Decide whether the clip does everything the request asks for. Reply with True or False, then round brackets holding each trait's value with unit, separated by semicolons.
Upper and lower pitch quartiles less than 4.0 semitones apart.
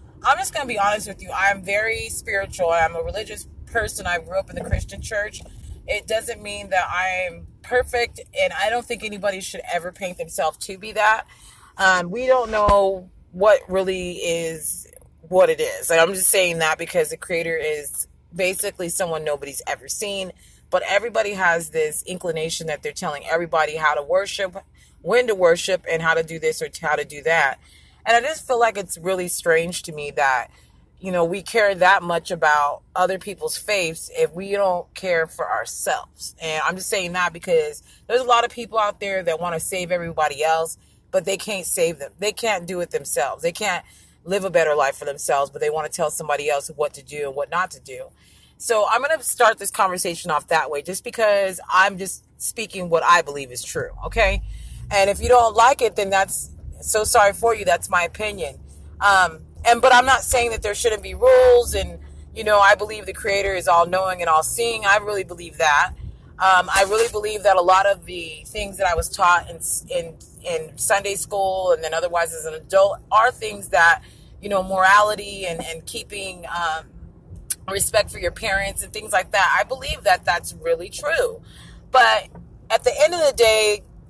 False (4.7 semitones)